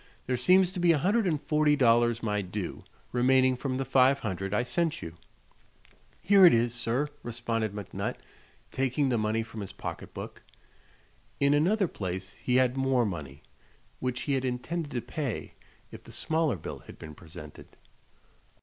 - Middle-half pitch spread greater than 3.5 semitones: Yes, average, 5.1 semitones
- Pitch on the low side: Yes, low, 125 Hz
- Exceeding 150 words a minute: Yes, average, 170 wpm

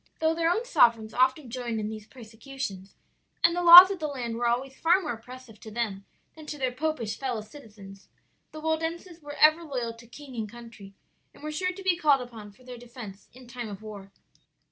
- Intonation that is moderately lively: No, wide, 5.8 semitones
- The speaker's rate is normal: No, fast, 210 wpm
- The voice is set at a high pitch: Yes, very high, 250 Hz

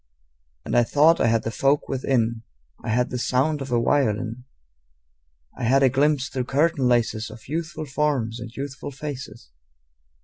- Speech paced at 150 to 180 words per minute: Yes, average, 165 wpm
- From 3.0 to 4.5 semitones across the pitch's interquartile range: Yes, average, 3.4 semitones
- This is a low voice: Yes, low, 130 Hz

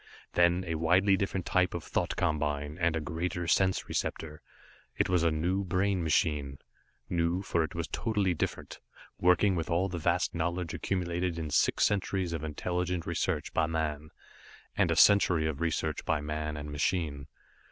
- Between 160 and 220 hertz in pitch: No, very low, 85 Hz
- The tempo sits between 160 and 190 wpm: Yes, average, 165 wpm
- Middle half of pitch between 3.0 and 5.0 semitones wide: No, narrow, 2.6 semitones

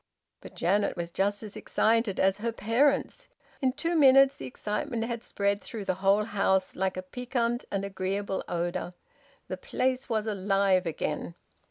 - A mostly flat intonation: No, average, 3.7 semitones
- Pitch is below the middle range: No, high, 205 Hz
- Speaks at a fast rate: No, average, 160 wpm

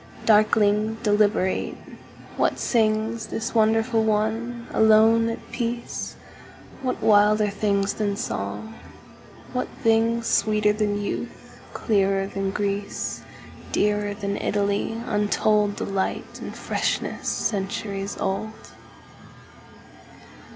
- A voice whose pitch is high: Yes, high, 210 Hz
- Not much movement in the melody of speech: Yes, narrow, 1.6 semitones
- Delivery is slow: Yes, slow, 80 wpm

